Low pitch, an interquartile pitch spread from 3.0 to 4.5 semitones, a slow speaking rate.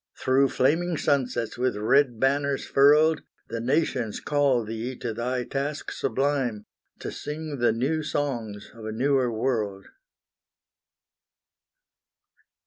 Yes: low, 130 Hz; average, 3.8 semitones; slow, 115 wpm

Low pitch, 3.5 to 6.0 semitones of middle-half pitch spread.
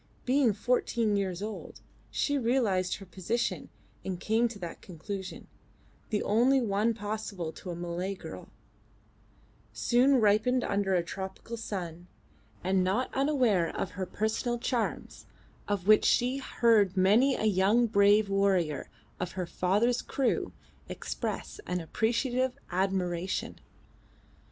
No: high, 205 Hz; average, 4.1 semitones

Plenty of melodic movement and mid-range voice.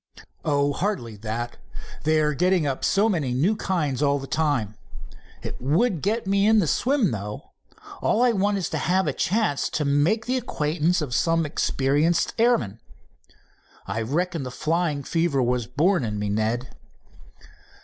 Yes: wide, 6.6 semitones; medium, 155 Hz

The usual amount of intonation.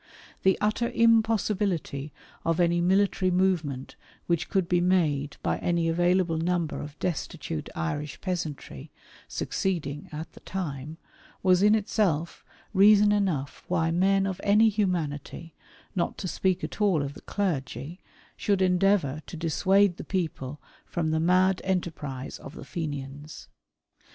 Yes: average, 4.2 semitones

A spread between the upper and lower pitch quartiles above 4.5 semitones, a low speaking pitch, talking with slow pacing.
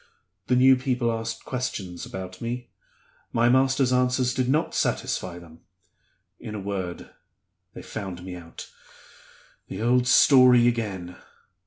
Yes: average, 5.1 semitones; low, 120 Hz; slow, 130 wpm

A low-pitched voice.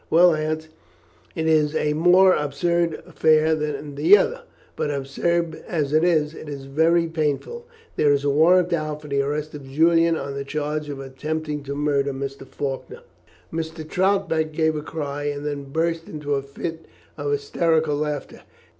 No: medium, 155 Hz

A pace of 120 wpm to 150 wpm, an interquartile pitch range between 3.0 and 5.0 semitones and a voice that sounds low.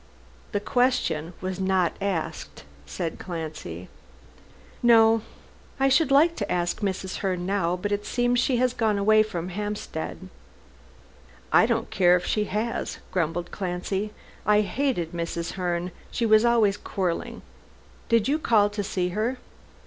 No: average, 140 wpm; average, 4.1 semitones; high, 200 Hz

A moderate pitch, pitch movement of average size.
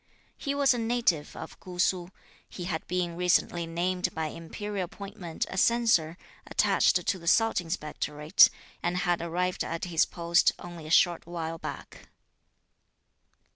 No: medium, 175 Hz; narrow, 2.1 semitones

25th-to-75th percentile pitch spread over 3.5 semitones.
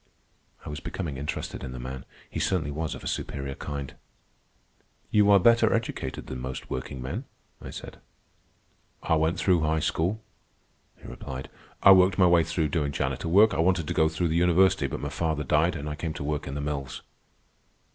Yes: average, 3.9 semitones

